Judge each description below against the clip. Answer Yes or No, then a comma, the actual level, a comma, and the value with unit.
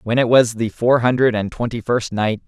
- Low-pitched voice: Yes, low, 115 Hz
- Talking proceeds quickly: Yes, fast, 240 wpm